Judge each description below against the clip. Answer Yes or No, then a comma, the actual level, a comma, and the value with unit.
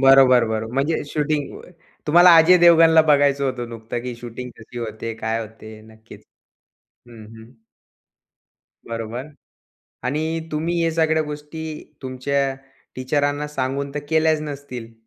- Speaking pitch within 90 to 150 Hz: Yes, low, 135 Hz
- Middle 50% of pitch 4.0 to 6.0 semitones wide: Yes, average, 4.6 semitones